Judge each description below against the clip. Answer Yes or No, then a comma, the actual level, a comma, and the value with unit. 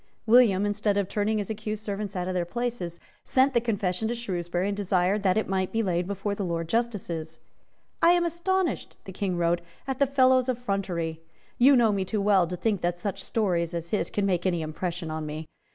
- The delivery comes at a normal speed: No, fast, 210 wpm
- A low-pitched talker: No, high, 200 Hz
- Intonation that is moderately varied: Yes, average, 4.2 semitones